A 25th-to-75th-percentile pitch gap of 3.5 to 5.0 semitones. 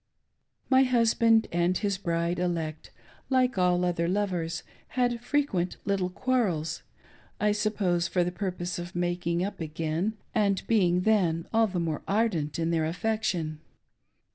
Yes: average, 4.2 semitones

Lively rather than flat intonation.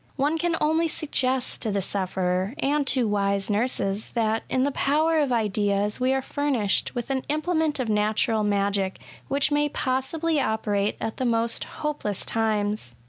Yes: wide, 5.7 semitones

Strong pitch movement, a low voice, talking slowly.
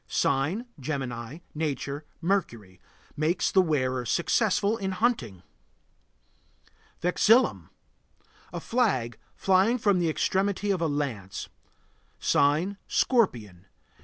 No: wide, 7.6 semitones; medium, 160 Hz; slow, 95 wpm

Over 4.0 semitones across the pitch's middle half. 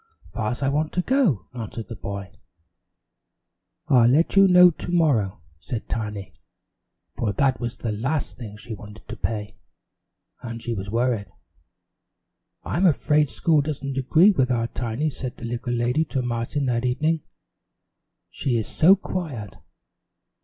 Yes: average, 5.3 semitones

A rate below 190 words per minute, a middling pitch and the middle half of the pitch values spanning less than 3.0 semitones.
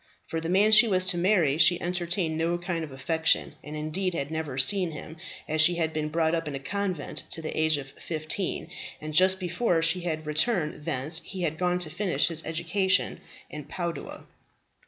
No: average, 200 wpm; medium, 165 Hz; narrow, 2.5 semitones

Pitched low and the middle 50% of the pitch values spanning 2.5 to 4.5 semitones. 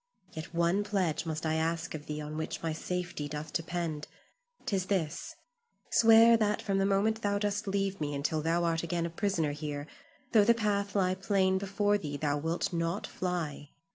No: medium, 175 Hz; average, 4.2 semitones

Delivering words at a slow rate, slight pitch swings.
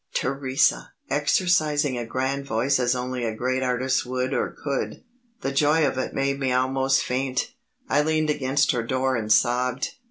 No: average, 165 wpm; narrow, 1.8 semitones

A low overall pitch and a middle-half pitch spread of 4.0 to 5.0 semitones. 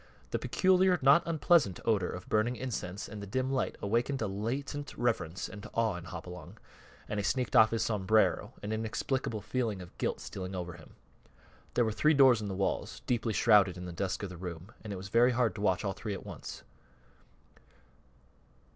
Yes: low, 110 Hz; average, 4.5 semitones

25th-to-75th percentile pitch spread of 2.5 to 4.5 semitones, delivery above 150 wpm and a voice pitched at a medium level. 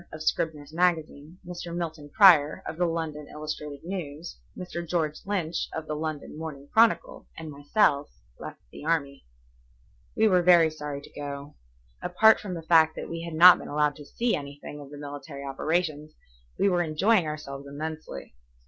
Yes: average, 2.9 semitones; average, 165 wpm; medium, 155 Hz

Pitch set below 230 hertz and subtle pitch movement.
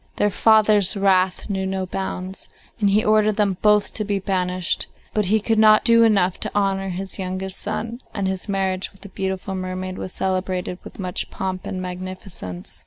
Yes: high, 190 Hz; narrow, 2.0 semitones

